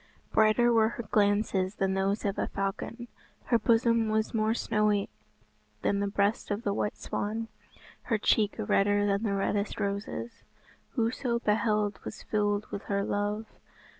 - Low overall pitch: No, high, 210 Hz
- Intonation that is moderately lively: No, narrow, 1.8 semitones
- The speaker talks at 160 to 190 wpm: No, average, 150 wpm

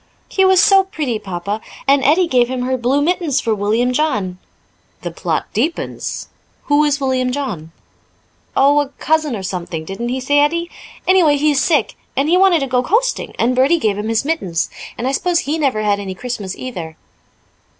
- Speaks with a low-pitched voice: No, very high, 265 Hz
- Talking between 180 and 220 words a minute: Yes, average, 190 wpm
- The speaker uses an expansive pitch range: Yes, wide, 6.0 semitones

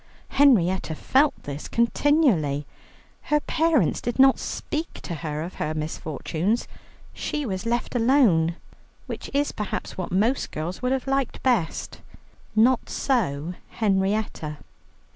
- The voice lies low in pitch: No, high, 215 Hz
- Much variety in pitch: Yes, wide, 8.6 semitones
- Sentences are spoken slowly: Yes, slow, 125 wpm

